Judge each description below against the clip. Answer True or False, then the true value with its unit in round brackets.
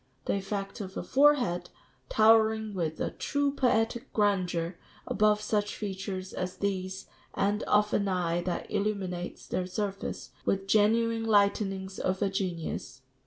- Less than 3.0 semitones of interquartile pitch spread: True (2.5 semitones)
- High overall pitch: True (200 Hz)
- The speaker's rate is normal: False (130 wpm)